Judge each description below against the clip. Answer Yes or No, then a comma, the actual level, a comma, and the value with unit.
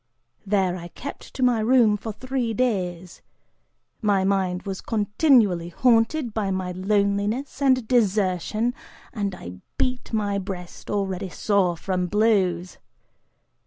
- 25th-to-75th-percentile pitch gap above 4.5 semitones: No, average, 3.6 semitones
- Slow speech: Yes, slow, 125 wpm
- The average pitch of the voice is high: Yes, high, 200 Hz